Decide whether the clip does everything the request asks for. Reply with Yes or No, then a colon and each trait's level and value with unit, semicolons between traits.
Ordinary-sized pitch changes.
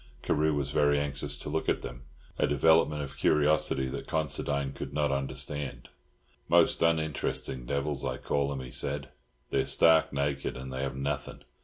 No: narrow, 1.4 semitones